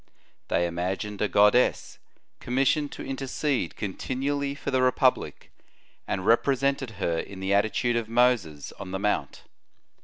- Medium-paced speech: No, slow, 130 wpm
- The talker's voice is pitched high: No, low, 115 Hz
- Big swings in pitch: Yes, wide, 5.7 semitones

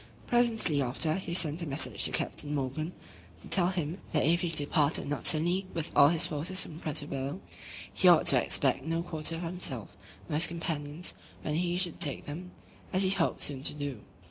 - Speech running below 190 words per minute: No, average, 195 wpm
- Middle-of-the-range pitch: Yes, medium, 160 Hz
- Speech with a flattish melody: No, average, 3.2 semitones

